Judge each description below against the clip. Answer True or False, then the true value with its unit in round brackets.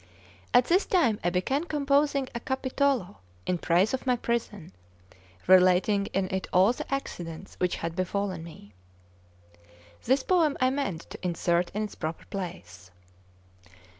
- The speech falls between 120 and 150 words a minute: True (140 wpm)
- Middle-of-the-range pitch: False (200 Hz)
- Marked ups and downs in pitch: True (6.9 semitones)